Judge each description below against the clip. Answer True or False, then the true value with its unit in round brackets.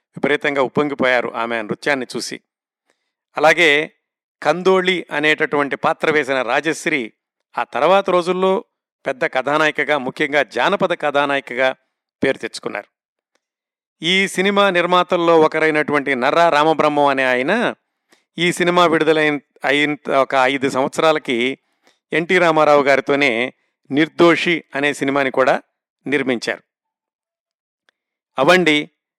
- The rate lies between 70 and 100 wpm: True (95 wpm)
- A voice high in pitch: False (150 Hz)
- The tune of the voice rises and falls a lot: False (3.9 semitones)